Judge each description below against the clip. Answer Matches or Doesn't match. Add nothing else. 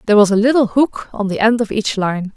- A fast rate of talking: Matches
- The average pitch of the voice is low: Doesn't match